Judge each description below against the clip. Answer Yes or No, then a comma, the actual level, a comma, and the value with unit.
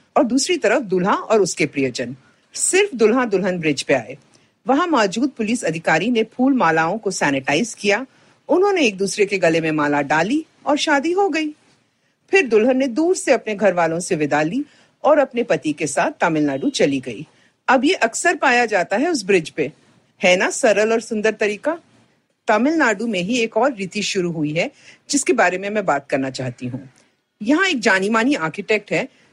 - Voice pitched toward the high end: Yes, high, 215 Hz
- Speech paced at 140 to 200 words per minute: Yes, average, 185 wpm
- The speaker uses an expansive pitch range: Yes, wide, 8.5 semitones